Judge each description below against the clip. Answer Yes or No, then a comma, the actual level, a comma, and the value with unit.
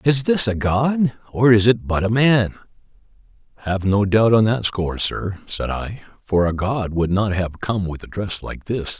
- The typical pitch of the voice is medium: No, low, 105 Hz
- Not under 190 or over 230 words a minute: Yes, fast, 205 wpm